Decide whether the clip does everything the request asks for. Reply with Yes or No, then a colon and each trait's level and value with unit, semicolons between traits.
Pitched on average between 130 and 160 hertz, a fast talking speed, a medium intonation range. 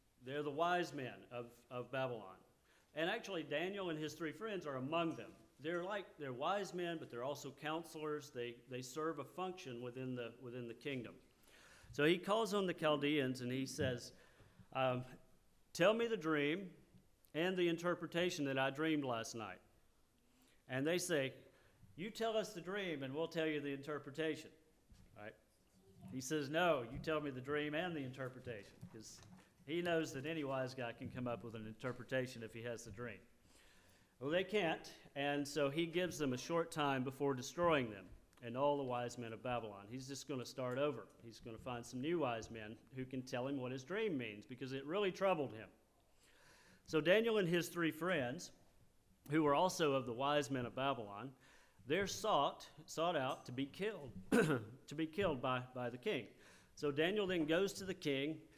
No: medium, 140 Hz; average, 190 wpm; average, 4.9 semitones